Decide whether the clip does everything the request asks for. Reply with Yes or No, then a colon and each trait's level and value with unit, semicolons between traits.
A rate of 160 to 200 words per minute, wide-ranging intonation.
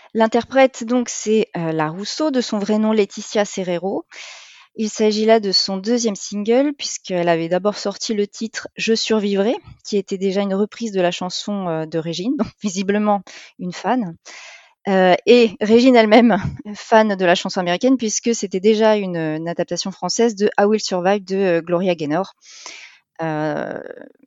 No: average, 165 wpm; average, 3.5 semitones